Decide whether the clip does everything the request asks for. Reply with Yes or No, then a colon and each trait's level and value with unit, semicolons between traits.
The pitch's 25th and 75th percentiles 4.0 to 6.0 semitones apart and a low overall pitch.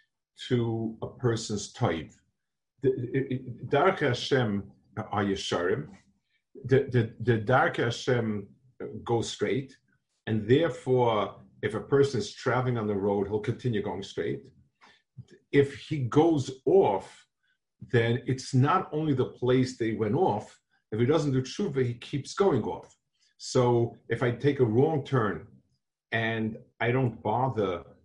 No: average, 3.3 semitones; low, 125 Hz